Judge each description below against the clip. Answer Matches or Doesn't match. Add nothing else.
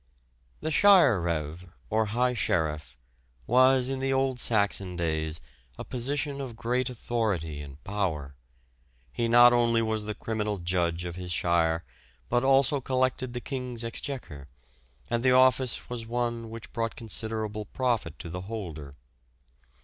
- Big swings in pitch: Matches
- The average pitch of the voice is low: Matches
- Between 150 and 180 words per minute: Doesn't match